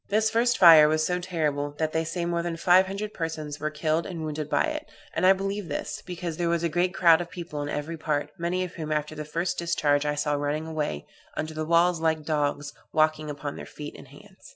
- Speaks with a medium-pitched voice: Yes, medium, 160 Hz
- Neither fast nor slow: No, fast, 235 wpm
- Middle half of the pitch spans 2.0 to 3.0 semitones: Yes, narrow, 2.5 semitones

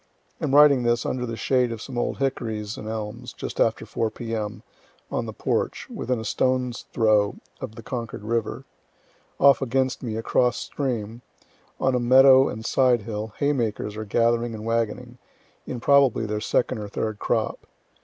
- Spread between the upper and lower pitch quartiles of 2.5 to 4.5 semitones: Yes, average, 2.8 semitones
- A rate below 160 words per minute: No, average, 165 wpm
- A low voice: Yes, low, 115 Hz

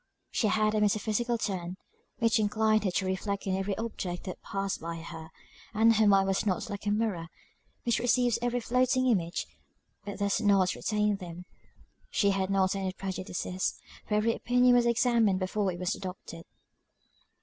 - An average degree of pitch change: Yes, average, 3.1 semitones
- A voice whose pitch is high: Yes, high, 200 Hz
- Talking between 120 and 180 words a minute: Yes, average, 170 wpm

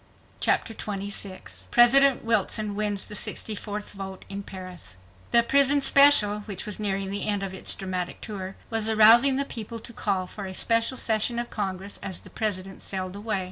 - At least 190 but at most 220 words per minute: No, average, 175 wpm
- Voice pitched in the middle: No, high, 205 Hz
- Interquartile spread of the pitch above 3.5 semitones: No, average, 2.9 semitones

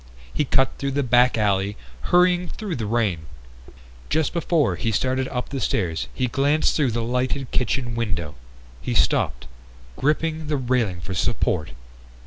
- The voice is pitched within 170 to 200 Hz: No, low, 125 Hz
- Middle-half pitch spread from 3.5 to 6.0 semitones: Yes, average, 5.0 semitones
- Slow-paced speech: No, average, 150 wpm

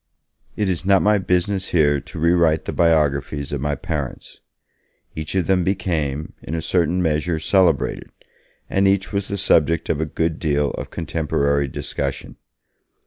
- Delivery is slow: No, average, 160 wpm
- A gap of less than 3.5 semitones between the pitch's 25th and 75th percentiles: No, average, 3.9 semitones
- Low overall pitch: Yes, very low, 80 Hz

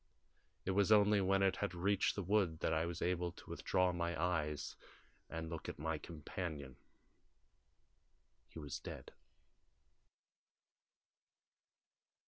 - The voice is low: Yes, very low, 85 Hz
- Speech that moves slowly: Yes, slow, 120 wpm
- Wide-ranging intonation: No, average, 3.2 semitones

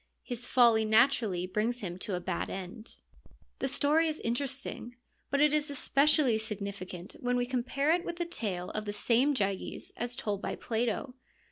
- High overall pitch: Yes, high, 240 Hz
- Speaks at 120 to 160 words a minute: No, average, 175 wpm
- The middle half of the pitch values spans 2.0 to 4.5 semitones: No, average, 5.0 semitones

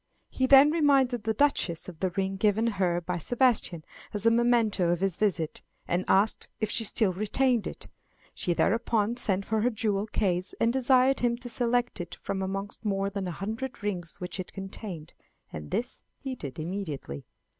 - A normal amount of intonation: Yes, average, 4.6 semitones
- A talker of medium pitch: No, high, 205 Hz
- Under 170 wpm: No, average, 180 wpm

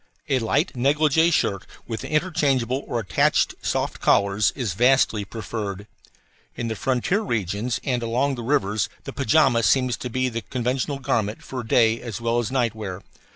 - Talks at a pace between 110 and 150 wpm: No, average, 160 wpm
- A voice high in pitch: No, low, 120 Hz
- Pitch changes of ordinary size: Yes, average, 3.4 semitones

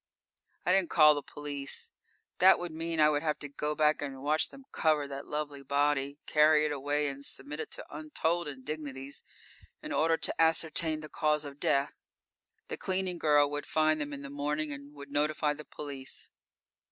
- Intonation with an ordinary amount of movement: No, narrow, 1.5 semitones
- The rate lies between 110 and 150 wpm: No, average, 185 wpm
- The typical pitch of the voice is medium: Yes, medium, 150 Hz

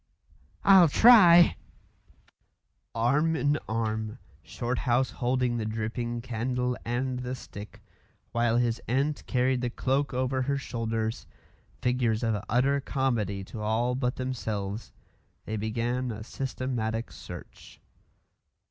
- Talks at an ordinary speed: No, slow, 115 wpm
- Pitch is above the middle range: No, low, 125 Hz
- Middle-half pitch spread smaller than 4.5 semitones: Yes, average, 2.7 semitones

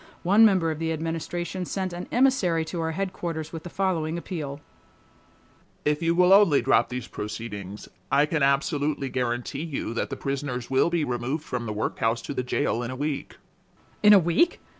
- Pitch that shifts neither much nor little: Yes, average, 4.9 semitones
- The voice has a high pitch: No, medium, 155 Hz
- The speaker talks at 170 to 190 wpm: Yes, average, 180 wpm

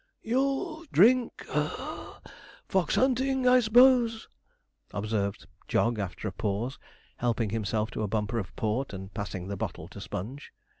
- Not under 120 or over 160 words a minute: Yes, average, 140 wpm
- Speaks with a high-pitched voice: No, low, 115 Hz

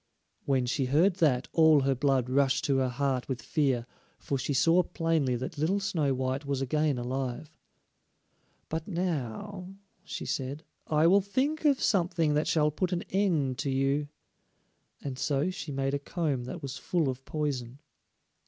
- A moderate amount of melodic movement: Yes, average, 3.8 semitones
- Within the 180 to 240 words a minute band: No, average, 165 wpm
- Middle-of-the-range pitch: Yes, medium, 145 Hz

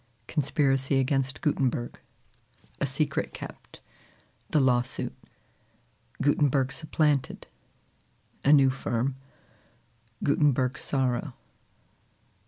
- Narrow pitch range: Yes, narrow, 1.9 semitones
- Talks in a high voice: No, low, 135 Hz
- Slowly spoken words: Yes, slow, 70 wpm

